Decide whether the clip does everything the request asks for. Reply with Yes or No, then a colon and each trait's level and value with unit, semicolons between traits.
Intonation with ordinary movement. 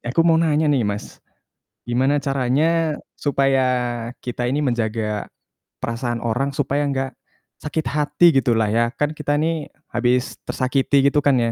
Yes: average, 3.5 semitones